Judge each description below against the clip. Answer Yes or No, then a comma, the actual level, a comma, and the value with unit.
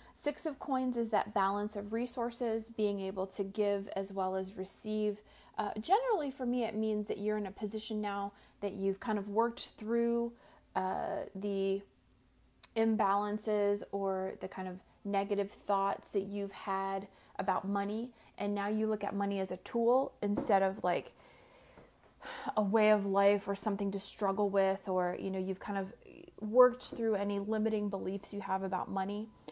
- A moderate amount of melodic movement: No, narrow, 2.2 semitones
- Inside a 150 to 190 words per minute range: Yes, average, 170 wpm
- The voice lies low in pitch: No, high, 205 Hz